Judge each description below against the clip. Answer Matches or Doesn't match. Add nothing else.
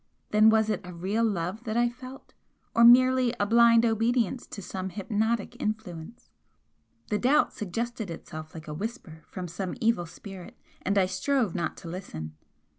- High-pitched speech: Matches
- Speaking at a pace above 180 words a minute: Doesn't match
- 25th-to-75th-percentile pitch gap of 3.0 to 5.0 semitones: Matches